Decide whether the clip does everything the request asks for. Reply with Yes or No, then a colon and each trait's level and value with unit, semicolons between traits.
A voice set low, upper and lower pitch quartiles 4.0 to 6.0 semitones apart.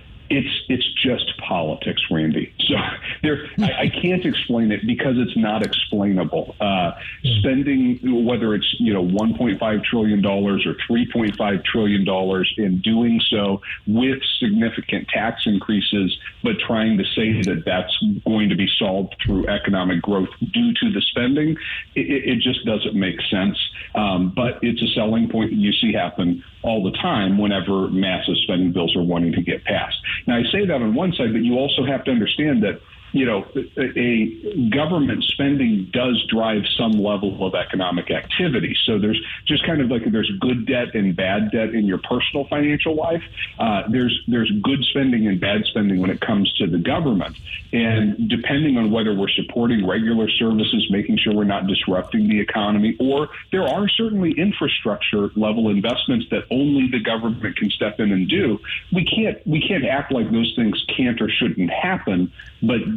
Yes: low, 110 Hz; average, 4.6 semitones